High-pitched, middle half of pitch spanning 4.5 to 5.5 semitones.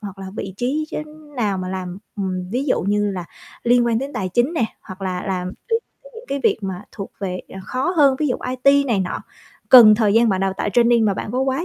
Yes: high, 215 Hz; average, 5.2 semitones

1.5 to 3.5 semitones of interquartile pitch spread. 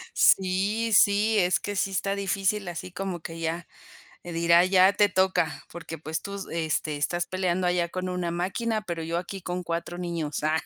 Yes: narrow, 2.5 semitones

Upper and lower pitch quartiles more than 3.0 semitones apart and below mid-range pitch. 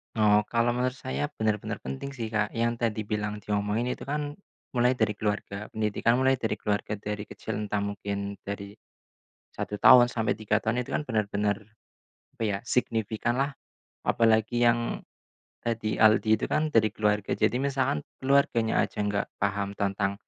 No: narrow, 2.5 semitones; low, 110 Hz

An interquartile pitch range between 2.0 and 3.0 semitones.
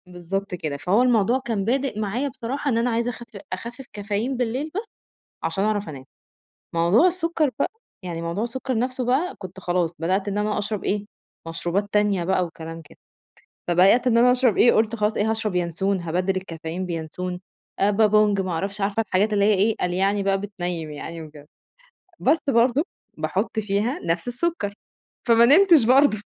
No: average, 4.7 semitones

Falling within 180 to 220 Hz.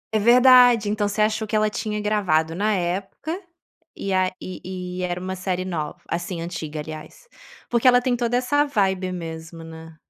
Yes: high, 190 Hz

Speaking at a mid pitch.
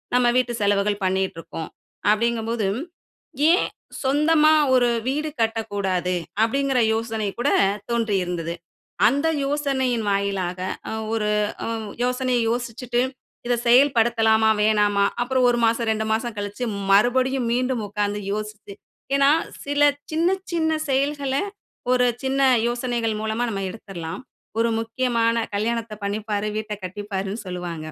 No: high, 230 Hz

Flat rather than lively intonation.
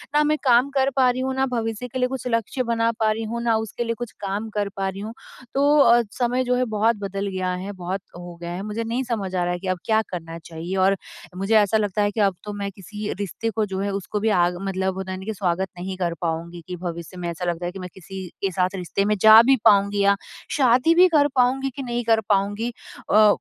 No: average, 3.8 semitones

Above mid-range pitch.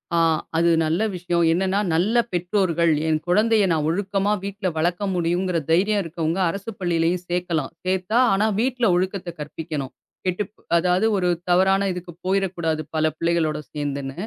No: medium, 180 Hz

